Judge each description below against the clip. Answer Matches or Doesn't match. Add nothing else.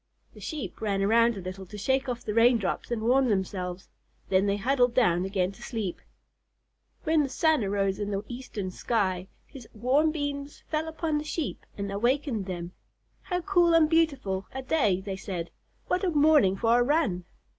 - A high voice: Matches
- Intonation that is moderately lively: Doesn't match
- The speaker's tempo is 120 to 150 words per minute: Doesn't match